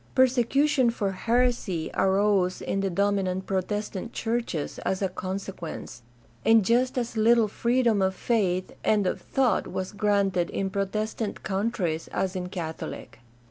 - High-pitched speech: Yes, high, 200 Hz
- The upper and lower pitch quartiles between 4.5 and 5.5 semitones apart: No, average, 3.7 semitones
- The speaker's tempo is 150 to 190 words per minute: No, slow, 135 wpm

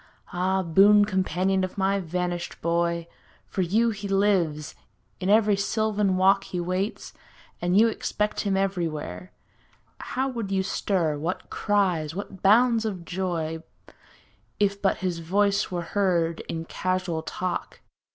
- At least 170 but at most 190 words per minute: No, slow, 135 wpm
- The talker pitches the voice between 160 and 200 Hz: Yes, high, 190 Hz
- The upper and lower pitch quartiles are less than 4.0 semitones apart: Yes, average, 2.8 semitones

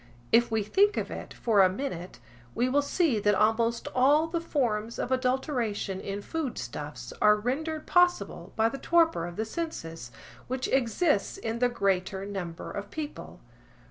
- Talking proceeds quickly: No, average, 165 wpm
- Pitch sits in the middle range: No, high, 230 Hz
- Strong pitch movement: Yes, wide, 6.1 semitones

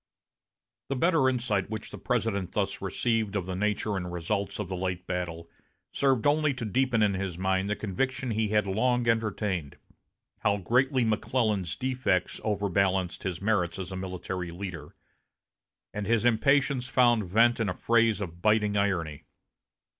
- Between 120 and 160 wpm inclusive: Yes, average, 155 wpm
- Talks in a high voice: No, low, 105 Hz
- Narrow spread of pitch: No, average, 4.0 semitones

